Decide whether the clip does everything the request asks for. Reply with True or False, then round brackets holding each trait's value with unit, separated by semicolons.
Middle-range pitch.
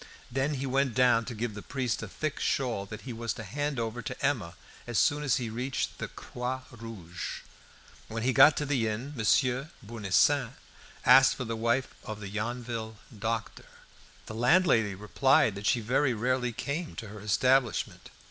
False (120 Hz)